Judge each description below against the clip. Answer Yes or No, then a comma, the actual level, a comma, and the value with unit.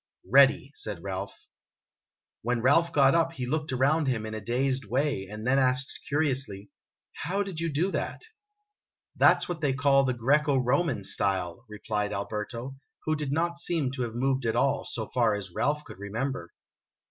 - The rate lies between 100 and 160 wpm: No, average, 185 wpm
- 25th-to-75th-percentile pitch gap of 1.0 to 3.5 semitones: No, average, 5.2 semitones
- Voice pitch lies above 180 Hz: No, low, 130 Hz